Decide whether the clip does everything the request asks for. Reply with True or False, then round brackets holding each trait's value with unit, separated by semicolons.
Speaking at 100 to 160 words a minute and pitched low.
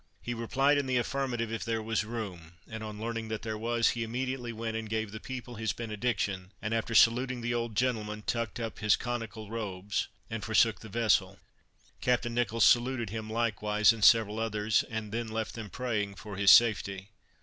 False (190 wpm; 115 Hz)